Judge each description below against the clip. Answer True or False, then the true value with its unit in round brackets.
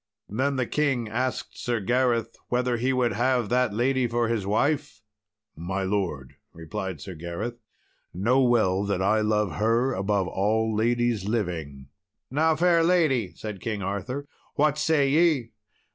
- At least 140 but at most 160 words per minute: True (145 wpm)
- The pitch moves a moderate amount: True (4.6 semitones)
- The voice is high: False (115 Hz)